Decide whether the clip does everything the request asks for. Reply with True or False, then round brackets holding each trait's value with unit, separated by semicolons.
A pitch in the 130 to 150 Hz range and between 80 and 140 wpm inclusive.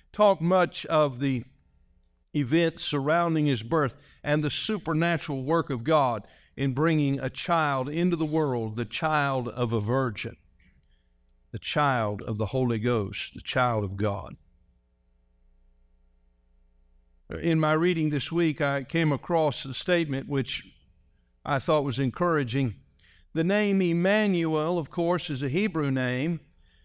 True (135 Hz; 135 wpm)